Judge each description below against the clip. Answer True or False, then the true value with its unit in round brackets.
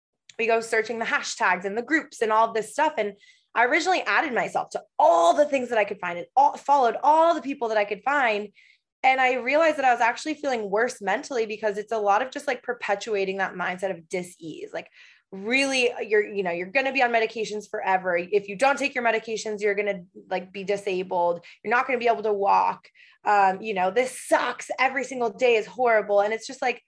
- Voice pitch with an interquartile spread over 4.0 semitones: True (4.4 semitones)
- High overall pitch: True (225 Hz)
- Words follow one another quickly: True (225 wpm)